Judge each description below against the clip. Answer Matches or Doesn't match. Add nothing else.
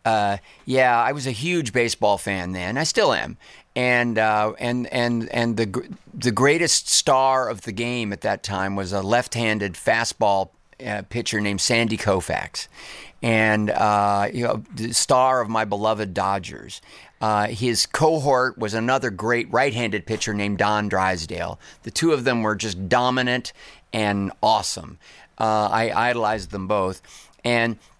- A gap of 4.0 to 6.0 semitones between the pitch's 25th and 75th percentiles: Doesn't match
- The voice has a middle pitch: Doesn't match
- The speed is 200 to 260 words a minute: Doesn't match